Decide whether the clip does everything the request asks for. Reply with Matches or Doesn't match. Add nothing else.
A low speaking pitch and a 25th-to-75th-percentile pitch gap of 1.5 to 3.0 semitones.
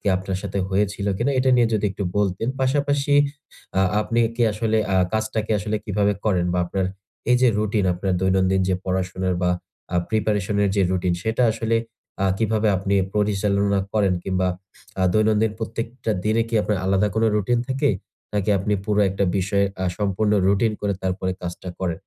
Matches